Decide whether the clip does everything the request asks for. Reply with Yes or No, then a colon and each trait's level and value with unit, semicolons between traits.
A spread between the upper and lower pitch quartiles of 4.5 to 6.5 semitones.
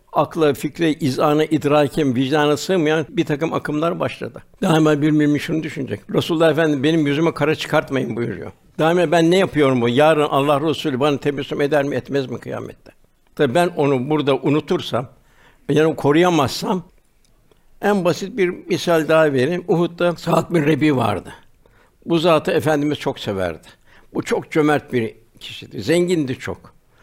No: average, 2.8 semitones